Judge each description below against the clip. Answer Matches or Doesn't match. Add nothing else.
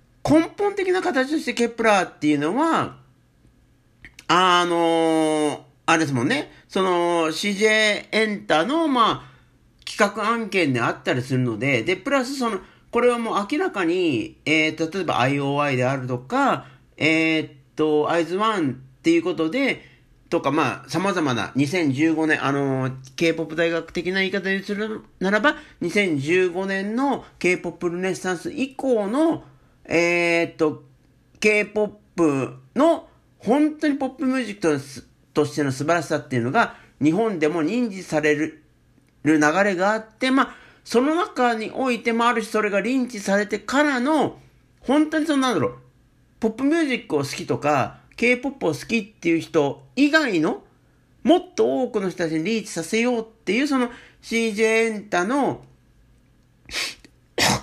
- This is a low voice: Doesn't match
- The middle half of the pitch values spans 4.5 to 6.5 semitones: Doesn't match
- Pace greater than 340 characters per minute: Doesn't match